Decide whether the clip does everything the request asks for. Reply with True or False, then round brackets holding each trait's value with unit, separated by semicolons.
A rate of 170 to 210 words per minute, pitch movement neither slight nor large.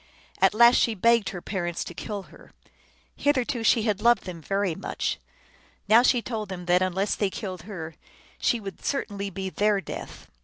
True (185 wpm; 3.4 semitones)